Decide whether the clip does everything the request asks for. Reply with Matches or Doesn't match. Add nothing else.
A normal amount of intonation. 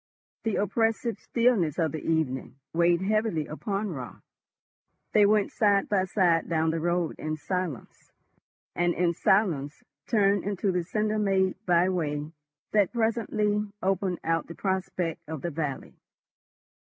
Matches